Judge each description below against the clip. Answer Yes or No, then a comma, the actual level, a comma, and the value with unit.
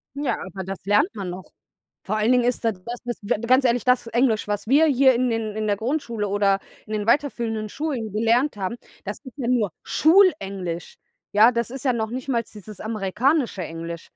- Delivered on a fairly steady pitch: No, average, 3.6 semitones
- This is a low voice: No, high, 225 Hz